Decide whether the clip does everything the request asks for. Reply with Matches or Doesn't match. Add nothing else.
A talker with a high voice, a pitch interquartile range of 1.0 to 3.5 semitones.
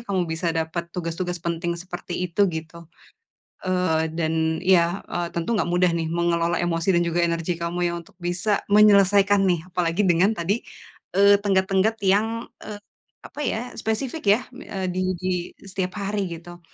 Doesn't match